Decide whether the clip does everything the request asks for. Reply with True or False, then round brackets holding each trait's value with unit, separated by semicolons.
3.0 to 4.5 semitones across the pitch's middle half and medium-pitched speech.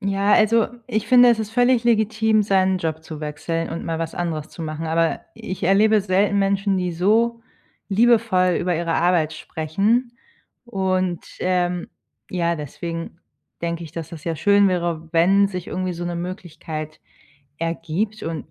True (3.6 semitones; 180 Hz)